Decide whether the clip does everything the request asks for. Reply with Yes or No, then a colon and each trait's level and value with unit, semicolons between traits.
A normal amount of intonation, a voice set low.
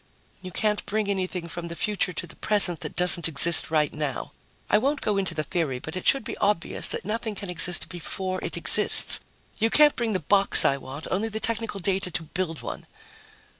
No: average, 4.0 semitones; medium, 185 Hz